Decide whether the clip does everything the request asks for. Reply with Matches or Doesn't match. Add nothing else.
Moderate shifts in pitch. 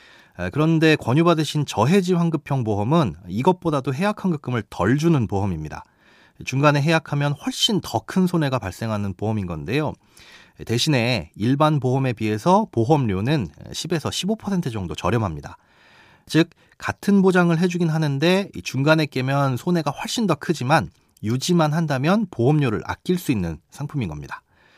Doesn't match